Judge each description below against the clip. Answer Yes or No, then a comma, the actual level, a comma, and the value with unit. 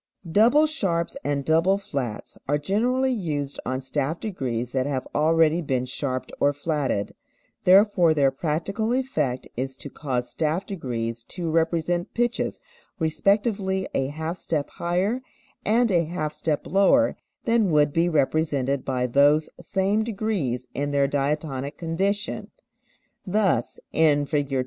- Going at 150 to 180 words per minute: No, slow, 135 wpm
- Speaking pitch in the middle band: Yes, medium, 160 Hz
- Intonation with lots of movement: Yes, wide, 5.7 semitones